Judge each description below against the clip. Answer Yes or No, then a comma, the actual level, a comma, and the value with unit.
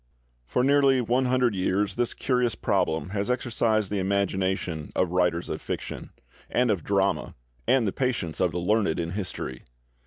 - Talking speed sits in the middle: Yes, average, 160 wpm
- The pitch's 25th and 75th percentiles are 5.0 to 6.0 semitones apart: Yes, wide, 5.4 semitones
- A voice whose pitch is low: Yes, low, 100 Hz